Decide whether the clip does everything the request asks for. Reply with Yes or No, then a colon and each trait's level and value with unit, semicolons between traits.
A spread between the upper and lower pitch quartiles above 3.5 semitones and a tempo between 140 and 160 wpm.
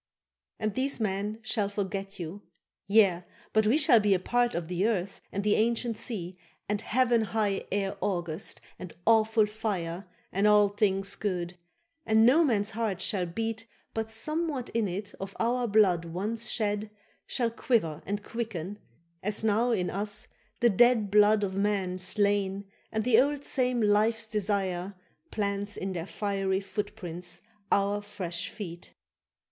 No: narrow, 2.6 semitones; average, 150 wpm